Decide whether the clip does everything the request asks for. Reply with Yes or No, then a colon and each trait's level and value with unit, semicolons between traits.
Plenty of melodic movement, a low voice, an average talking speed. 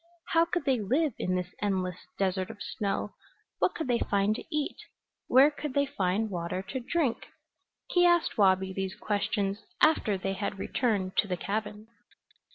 No: wide, 5.8 semitones; high, 210 Hz; average, 165 wpm